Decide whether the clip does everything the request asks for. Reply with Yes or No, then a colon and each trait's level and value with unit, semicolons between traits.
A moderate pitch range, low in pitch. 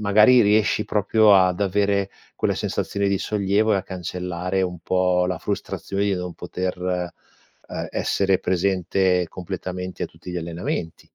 No: narrow, 1.8 semitones; very low, 95 Hz